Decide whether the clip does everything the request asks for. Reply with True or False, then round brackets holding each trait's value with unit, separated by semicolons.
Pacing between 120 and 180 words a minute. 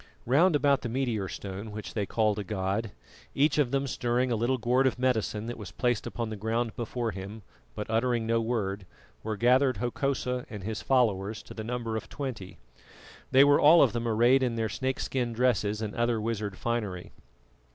False (190 wpm)